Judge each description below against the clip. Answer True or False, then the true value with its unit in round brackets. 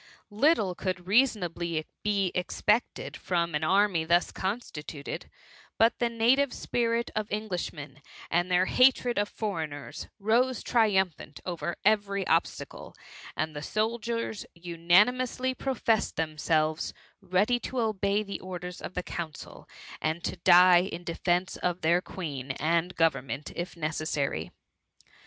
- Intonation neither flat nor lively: True (4.6 semitones)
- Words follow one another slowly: True (125 wpm)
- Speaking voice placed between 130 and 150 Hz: False (185 Hz)